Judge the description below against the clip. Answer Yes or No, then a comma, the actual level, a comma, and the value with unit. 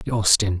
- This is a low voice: Yes, low, 100 Hz